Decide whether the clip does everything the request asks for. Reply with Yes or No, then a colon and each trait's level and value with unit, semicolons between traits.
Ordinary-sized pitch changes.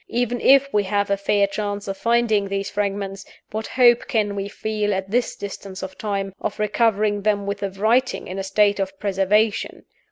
No: narrow, 1.7 semitones